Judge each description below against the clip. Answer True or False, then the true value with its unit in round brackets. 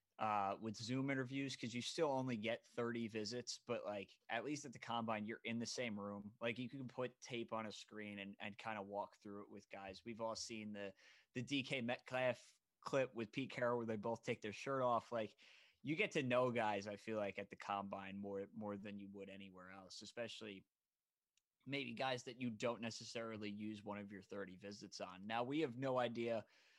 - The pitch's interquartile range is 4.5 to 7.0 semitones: False (3.2 semitones)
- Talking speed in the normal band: False (215 wpm)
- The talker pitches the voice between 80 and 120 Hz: True (115 Hz)